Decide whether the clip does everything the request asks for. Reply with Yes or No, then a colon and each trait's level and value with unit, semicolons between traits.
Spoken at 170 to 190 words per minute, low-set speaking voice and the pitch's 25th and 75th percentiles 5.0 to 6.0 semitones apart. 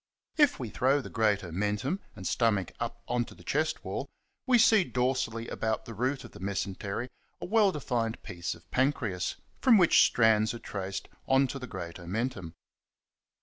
Yes: average, 180 wpm; low, 115 Hz; wide, 5.4 semitones